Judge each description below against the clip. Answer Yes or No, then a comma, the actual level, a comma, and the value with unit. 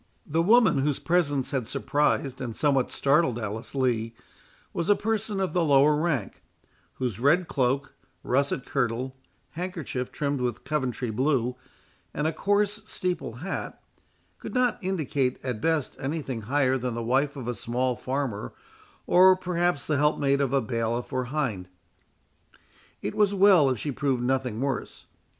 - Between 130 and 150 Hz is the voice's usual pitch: Yes, medium, 140 Hz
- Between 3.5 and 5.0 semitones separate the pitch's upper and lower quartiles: Yes, average, 4.7 semitones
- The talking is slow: No, average, 155 wpm